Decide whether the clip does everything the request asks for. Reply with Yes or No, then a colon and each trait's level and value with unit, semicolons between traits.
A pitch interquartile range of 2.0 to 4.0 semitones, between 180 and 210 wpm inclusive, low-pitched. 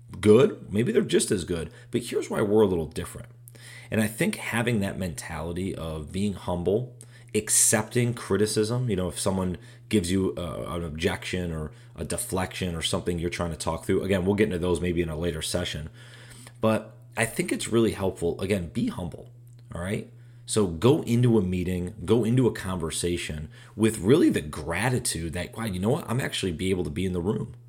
No: average, 5.2 semitones; average, 195 wpm; low, 105 Hz